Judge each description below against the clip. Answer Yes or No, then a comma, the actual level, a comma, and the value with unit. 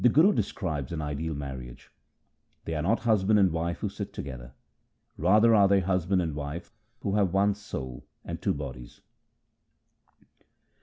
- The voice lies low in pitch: Yes, very low, 85 Hz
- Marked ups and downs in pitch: Yes, wide, 5.7 semitones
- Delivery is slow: No, average, 160 wpm